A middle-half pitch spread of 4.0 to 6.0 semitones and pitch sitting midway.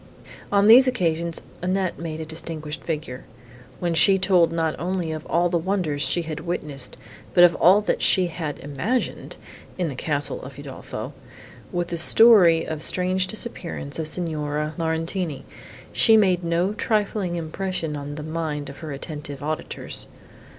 No: average, 3.2 semitones; medium, 165 Hz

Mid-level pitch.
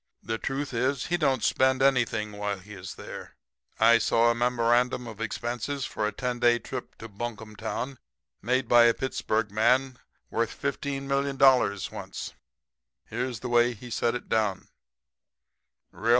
No: low, 120 Hz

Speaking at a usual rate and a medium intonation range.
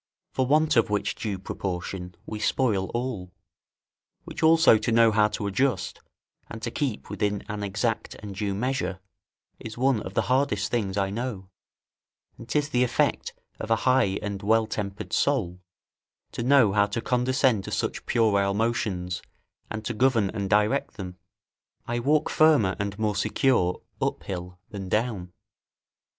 Yes: average, 160 wpm; average, 4.0 semitones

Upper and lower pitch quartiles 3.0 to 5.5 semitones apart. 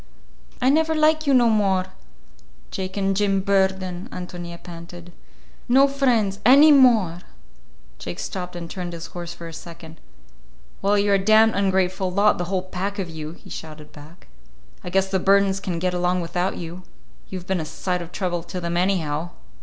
No: narrow, 2.5 semitones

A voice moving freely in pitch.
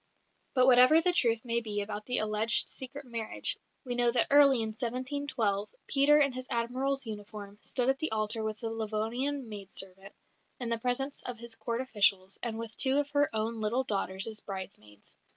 No: average, 3.4 semitones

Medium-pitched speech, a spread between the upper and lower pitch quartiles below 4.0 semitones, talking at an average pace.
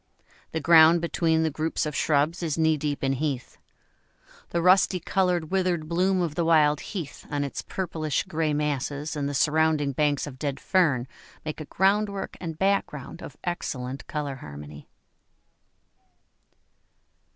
Yes: medium, 155 Hz; average, 3.0 semitones; average, 145 wpm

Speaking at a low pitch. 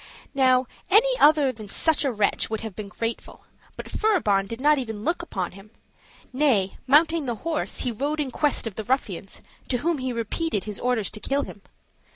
No: very high, 255 Hz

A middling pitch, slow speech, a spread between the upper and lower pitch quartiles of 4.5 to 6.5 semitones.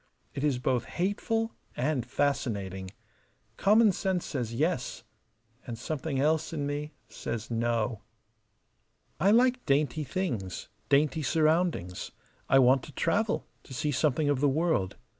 Yes: medium, 145 Hz; slow, 130 wpm; average, 5.1 semitones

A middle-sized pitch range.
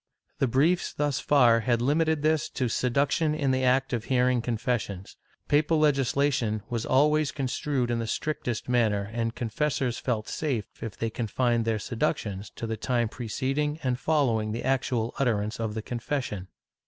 Yes: average, 3.6 semitones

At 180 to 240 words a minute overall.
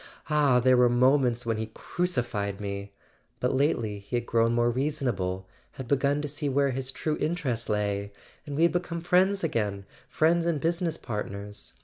Yes: average, 185 wpm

